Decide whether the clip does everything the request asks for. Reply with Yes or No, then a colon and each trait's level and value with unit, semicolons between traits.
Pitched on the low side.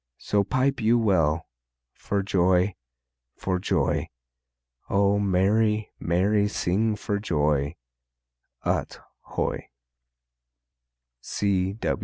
Yes: low, 100 Hz